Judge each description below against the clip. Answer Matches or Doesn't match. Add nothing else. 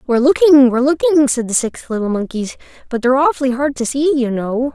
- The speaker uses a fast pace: Matches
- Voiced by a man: Doesn't match